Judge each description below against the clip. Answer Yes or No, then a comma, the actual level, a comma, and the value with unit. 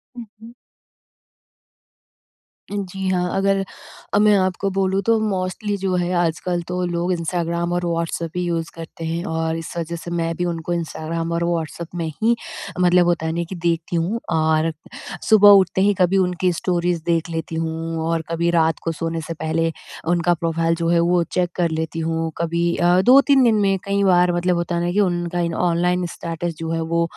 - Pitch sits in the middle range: Yes, medium, 170 Hz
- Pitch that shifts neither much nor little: No, narrow, 1.7 semitones